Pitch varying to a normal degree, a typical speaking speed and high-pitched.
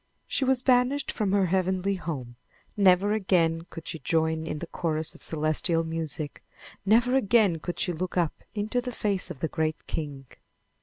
No: average, 4.5 semitones; average, 170 wpm; medium, 180 Hz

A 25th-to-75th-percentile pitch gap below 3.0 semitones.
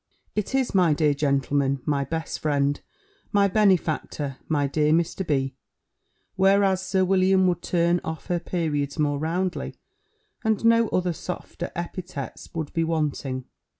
No: average, 4.5 semitones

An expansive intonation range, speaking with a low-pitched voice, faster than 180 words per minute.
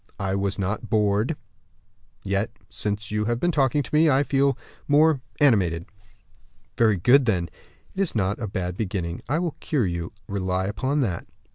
No: wide, 6.4 semitones; low, 105 Hz; average, 165 wpm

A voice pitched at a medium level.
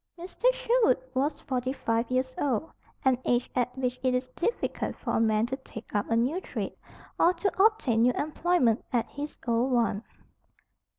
No: very high, 255 Hz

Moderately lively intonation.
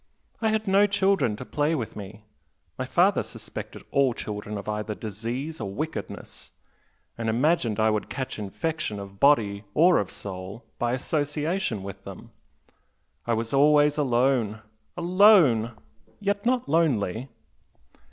No: wide, 7.1 semitones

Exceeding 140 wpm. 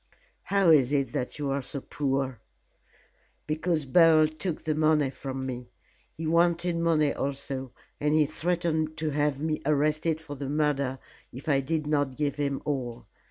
Yes: average, 160 wpm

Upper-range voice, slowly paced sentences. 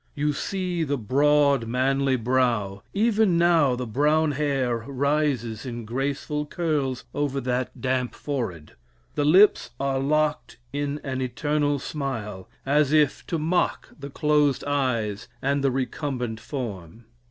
No: medium, 140 Hz; slow, 130 wpm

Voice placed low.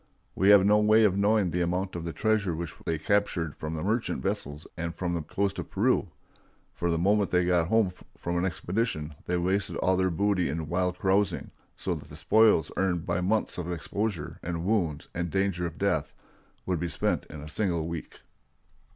Yes: very low, 90 Hz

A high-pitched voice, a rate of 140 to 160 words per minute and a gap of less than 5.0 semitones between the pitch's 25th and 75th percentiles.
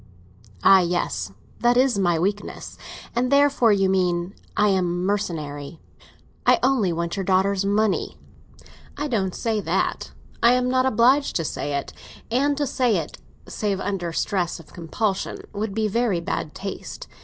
No: high, 200 Hz; average, 150 wpm; average, 5.3 semitones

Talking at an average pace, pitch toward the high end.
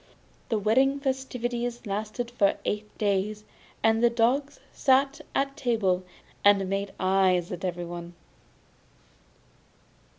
No: slow, 105 wpm; high, 215 Hz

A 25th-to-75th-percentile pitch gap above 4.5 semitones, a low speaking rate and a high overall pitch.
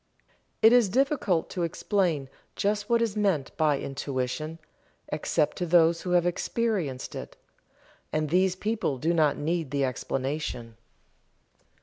No: wide, 5.5 semitones; slow, 130 wpm; medium, 165 Hz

